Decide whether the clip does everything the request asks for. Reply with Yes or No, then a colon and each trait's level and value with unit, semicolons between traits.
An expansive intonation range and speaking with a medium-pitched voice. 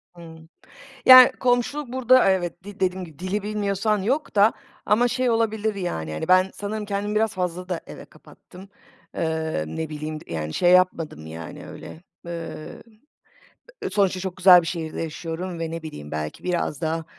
No: average, 4.4 semitones; medium, 180 Hz